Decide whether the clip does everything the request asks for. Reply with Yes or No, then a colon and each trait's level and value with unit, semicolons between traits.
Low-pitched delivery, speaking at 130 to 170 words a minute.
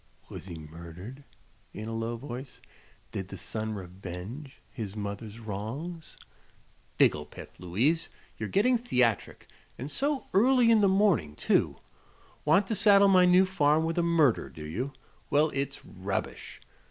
Yes: low, 130 Hz; average, 140 wpm